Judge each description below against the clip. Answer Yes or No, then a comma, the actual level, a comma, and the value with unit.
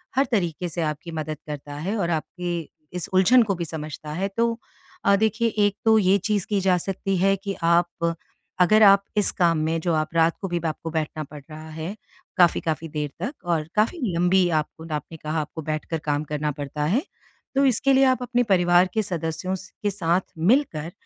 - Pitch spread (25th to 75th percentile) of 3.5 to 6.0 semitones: Yes, average, 4.0 semitones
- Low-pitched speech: No, medium, 175 Hz